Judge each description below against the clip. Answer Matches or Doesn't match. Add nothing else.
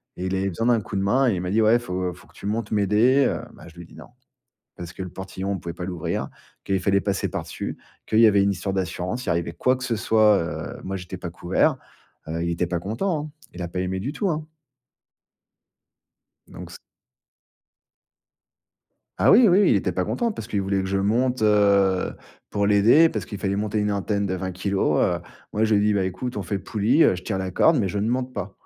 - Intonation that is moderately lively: Matches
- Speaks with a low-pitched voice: Matches